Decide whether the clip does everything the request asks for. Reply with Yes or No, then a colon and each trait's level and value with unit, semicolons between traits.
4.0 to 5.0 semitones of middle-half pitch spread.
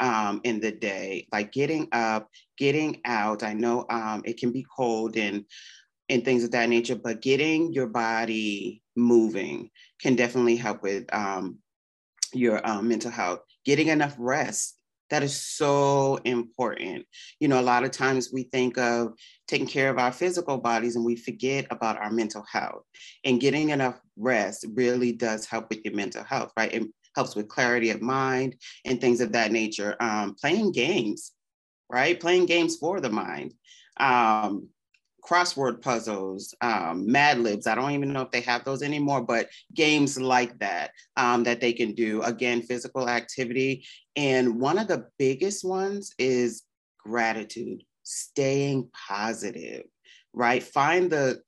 No: average, 2.9 semitones